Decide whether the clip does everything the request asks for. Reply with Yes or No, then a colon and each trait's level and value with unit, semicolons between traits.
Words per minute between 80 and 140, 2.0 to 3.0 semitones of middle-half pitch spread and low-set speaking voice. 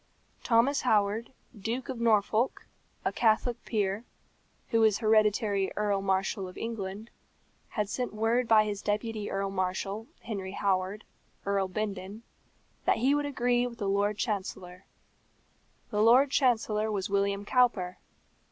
No: slow, 135 wpm; average, 2.7 semitones; high, 210 Hz